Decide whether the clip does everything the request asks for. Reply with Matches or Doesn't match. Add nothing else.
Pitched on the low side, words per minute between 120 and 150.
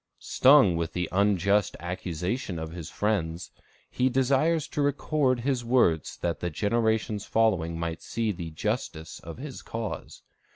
Matches